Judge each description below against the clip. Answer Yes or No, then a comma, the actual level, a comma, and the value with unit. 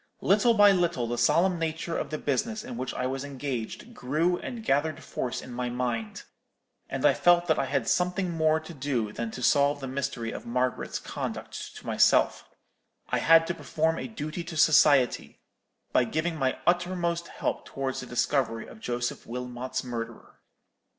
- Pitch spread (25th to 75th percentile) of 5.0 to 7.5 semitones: Yes, average, 5.3 semitones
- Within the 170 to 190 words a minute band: Yes, average, 175 wpm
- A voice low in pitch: No, medium, 145 Hz